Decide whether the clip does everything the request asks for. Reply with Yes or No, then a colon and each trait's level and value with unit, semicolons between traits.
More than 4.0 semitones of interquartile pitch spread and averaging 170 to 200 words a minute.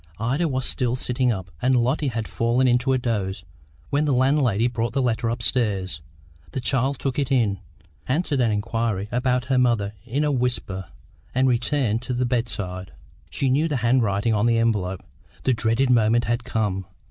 No: average, 2.9 semitones; average, 175 wpm